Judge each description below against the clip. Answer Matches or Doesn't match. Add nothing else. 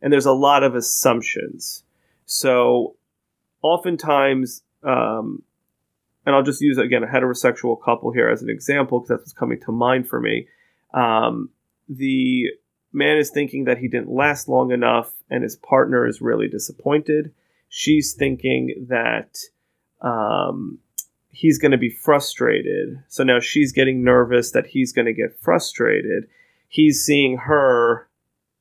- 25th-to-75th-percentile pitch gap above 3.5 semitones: Doesn't match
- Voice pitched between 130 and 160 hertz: Matches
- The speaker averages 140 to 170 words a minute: Matches